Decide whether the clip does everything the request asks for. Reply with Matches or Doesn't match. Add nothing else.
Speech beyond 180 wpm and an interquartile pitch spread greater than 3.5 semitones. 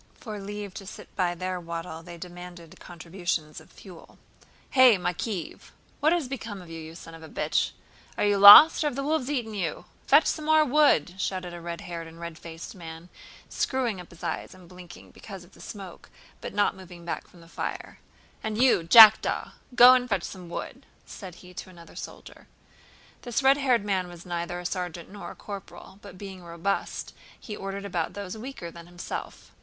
Matches